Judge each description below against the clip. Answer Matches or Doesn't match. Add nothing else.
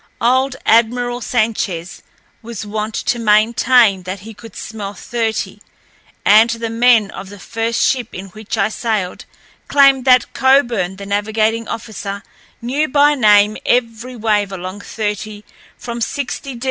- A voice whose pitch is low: Doesn't match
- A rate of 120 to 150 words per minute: Matches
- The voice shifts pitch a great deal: Doesn't match